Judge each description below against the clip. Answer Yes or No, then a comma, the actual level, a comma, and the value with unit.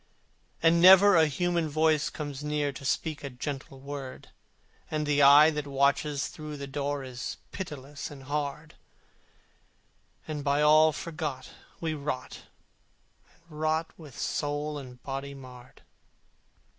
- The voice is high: No, medium, 145 Hz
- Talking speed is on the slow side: Yes, slow, 130 wpm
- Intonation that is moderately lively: No, narrow, 2.0 semitones